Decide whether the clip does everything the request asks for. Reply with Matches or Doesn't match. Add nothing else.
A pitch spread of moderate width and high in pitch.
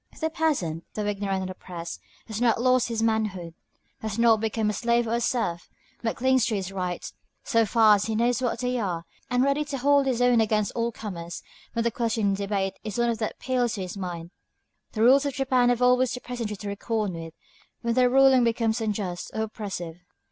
Matches